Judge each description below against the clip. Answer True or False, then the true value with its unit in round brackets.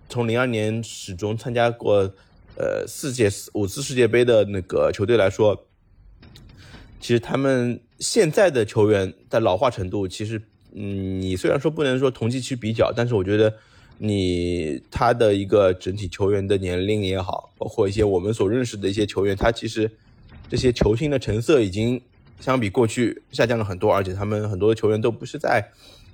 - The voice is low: True (105 Hz)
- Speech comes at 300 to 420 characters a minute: False (275 characters per minute)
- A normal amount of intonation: True (3.3 semitones)